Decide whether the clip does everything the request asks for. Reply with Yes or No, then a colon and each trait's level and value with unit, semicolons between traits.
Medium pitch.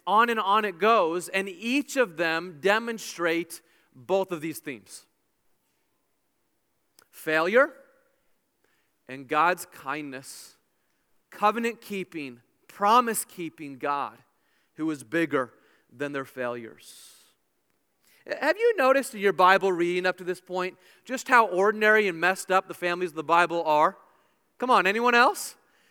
Yes: medium, 180 Hz